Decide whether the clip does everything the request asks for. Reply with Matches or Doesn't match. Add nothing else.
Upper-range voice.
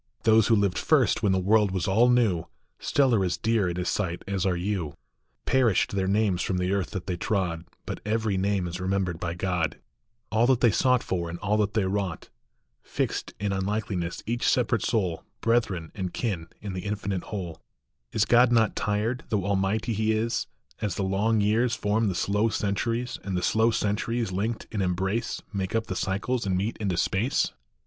Doesn't match